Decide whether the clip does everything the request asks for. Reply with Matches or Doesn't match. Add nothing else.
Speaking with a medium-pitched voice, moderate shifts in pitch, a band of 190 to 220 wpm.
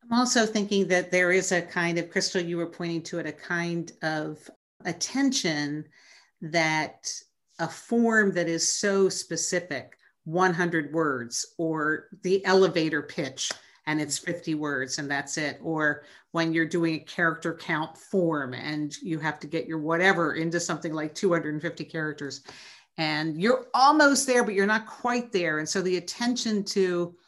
Doesn't match